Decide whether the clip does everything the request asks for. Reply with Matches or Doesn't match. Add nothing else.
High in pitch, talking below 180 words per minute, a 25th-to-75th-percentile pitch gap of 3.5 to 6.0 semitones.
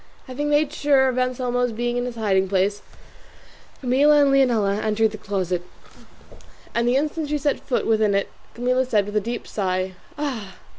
Matches